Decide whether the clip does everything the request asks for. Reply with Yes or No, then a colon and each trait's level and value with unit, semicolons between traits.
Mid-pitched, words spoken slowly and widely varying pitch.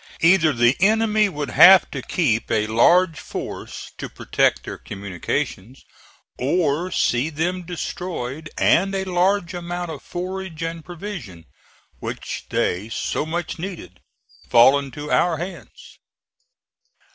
Yes: medium, 165 Hz; slow, 125 wpm; wide, 5.7 semitones